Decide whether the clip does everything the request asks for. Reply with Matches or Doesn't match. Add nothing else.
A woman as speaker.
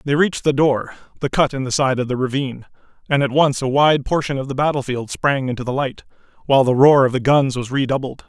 Doesn't match